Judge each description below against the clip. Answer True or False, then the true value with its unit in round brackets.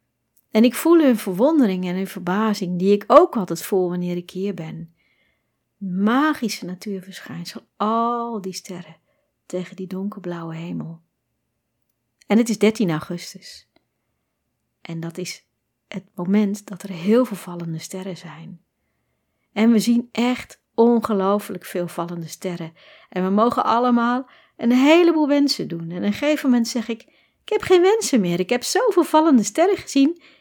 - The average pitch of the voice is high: True (200 Hz)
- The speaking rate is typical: True (150 wpm)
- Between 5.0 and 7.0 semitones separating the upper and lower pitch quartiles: True (5.4 semitones)